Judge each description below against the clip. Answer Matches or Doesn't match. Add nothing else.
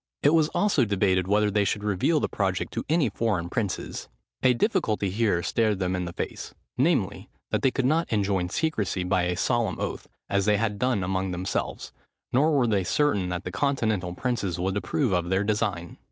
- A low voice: Matches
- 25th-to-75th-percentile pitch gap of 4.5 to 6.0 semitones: Matches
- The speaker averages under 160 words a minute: Doesn't match